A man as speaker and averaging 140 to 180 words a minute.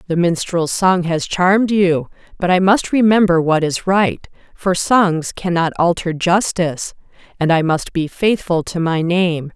No: female; average, 165 wpm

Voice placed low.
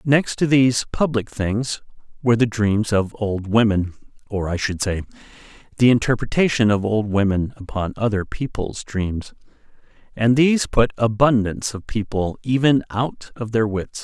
Yes: low, 110 Hz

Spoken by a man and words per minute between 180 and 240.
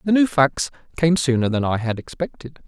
Yes: male; average, 200 wpm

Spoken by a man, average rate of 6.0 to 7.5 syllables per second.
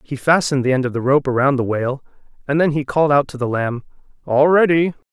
Yes: male; 6.4 syllables/s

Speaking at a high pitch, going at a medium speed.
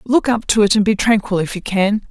No: high, 210 Hz; fast, 285 wpm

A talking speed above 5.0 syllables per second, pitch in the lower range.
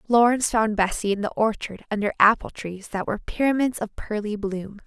No: 5.5 syllables/s; high, 215 Hz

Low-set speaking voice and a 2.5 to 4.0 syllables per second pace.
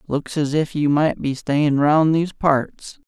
No: medium, 150 Hz; 3.8 syllables/s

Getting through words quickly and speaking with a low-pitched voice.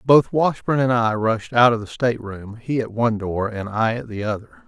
Yes: fast, 245 wpm; low, 115 Hz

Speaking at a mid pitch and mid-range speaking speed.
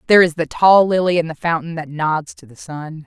No: medium, 165 Hz; fast, 255 wpm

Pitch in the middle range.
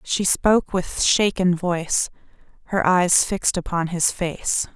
Yes: medium, 180 Hz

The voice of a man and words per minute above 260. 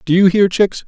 Yes: male; fast, 275 wpm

